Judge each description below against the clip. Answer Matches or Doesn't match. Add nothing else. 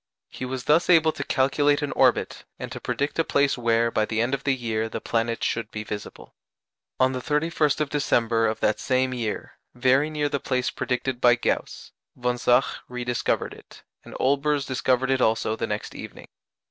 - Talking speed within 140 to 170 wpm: Doesn't match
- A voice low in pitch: Matches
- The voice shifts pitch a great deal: Doesn't match